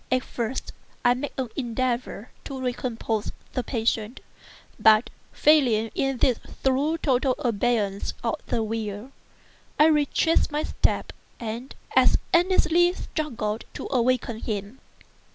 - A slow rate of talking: Yes, slow, 120 wpm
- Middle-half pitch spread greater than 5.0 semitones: No, average, 3.4 semitones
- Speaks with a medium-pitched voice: No, high, 245 Hz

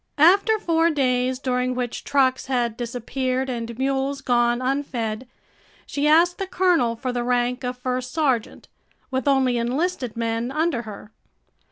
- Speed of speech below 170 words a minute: Yes, average, 145 wpm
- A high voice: Yes, very high, 255 Hz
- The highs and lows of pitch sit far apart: No, narrow, 2.5 semitones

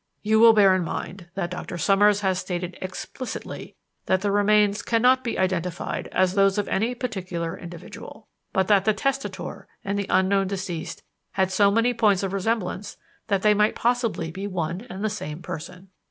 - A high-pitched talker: Yes, high, 195 Hz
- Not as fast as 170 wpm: No, average, 175 wpm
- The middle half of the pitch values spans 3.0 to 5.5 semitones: No, narrow, 2.4 semitones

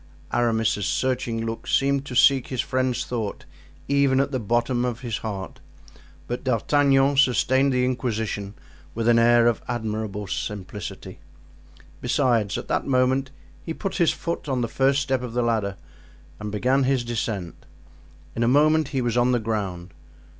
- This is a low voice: Yes, low, 120 Hz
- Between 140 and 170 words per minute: Yes, average, 160 wpm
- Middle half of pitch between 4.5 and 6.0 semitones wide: No, average, 3.1 semitones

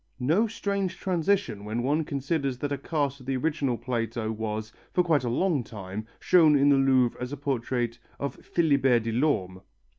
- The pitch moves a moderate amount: Yes, average, 4.8 semitones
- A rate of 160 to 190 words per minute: Yes, average, 175 wpm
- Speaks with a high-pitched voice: No, low, 135 Hz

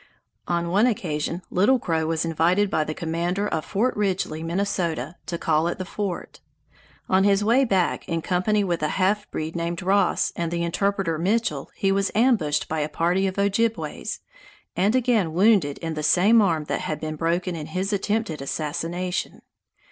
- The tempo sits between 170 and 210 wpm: Yes, average, 175 wpm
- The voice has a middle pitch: Yes, medium, 180 Hz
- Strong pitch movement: No, average, 3.6 semitones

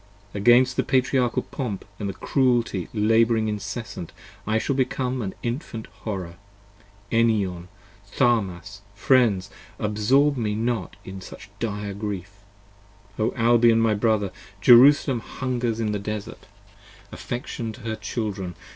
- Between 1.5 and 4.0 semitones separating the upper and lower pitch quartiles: Yes, average, 3.1 semitones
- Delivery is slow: Yes, slow, 120 wpm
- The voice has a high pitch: No, low, 110 Hz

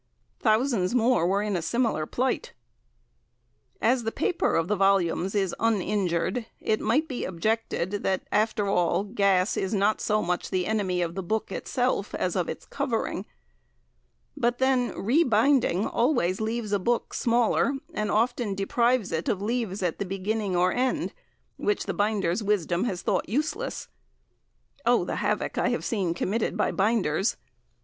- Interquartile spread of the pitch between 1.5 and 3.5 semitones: No, average, 4.1 semitones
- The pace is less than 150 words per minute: No, average, 155 wpm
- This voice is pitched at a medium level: No, high, 210 Hz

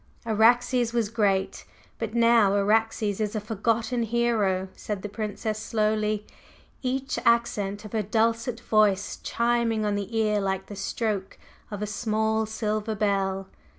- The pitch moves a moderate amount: No, narrow, 2.0 semitones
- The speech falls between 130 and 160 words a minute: Yes, average, 140 wpm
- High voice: Yes, high, 215 Hz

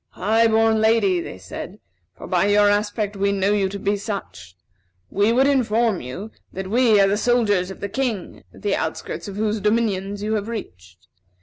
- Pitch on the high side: Yes, high, 205 Hz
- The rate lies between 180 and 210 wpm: Yes, average, 185 wpm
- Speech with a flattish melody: Yes, narrow, 2.3 semitones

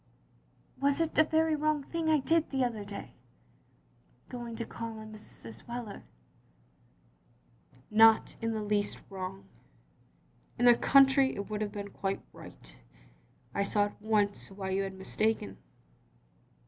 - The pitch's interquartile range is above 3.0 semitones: Yes, average, 4.8 semitones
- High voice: Yes, high, 220 Hz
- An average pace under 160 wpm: Yes, average, 145 wpm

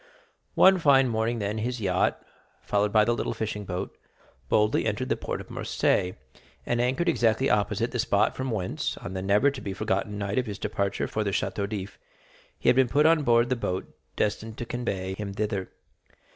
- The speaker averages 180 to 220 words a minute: Yes, average, 195 wpm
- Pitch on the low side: Yes, low, 110 Hz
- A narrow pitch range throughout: No, average, 3.4 semitones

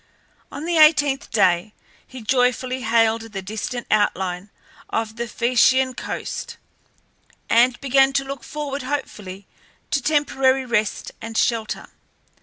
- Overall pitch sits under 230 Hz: No, high, 245 Hz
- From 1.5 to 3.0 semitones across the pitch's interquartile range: No, average, 3.6 semitones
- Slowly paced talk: Yes, slow, 120 wpm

